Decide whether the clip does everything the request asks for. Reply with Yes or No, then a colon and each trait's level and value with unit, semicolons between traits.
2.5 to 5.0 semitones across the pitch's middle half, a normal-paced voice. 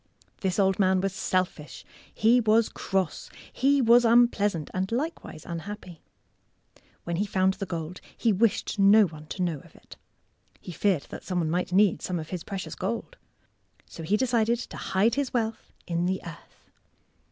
Yes: average, 4.1 semitones; average, 170 wpm